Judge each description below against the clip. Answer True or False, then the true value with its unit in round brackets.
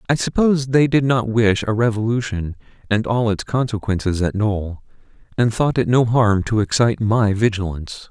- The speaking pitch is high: False (110 Hz)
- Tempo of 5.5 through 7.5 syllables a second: False (5.1 syllables/s)